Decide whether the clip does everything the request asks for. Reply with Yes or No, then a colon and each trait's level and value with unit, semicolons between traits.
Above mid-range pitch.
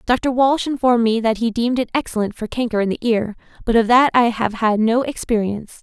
Yes: high, 230 Hz